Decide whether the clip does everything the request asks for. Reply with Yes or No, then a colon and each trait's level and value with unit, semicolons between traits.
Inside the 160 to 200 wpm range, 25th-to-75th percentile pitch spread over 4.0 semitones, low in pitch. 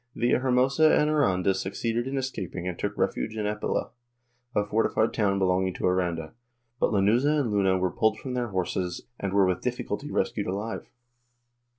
Yes: average, 165 wpm; average, 4.5 semitones; low, 105 Hz